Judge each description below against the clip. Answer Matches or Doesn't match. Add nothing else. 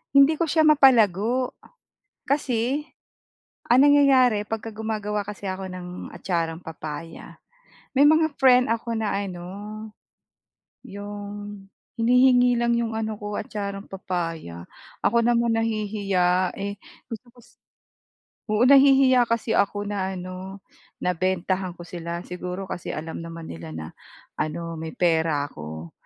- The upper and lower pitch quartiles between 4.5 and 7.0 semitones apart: Matches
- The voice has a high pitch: Matches